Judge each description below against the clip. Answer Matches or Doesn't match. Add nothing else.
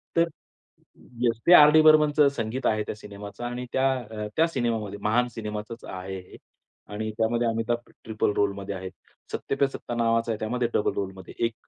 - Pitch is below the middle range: Matches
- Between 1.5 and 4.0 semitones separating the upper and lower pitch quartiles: Matches